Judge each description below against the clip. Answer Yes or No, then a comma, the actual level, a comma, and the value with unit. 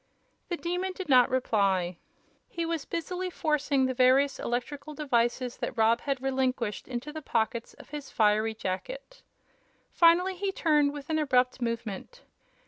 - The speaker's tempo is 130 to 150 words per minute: Yes, average, 145 wpm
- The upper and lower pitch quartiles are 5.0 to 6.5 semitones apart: Yes, average, 5.3 semitones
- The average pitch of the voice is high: Yes, very high, 270 Hz